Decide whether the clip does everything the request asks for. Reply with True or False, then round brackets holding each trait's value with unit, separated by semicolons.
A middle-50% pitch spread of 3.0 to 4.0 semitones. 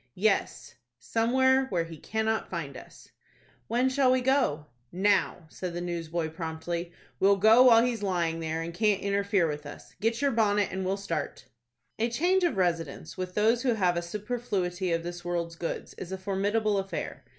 False (4.8 semitones)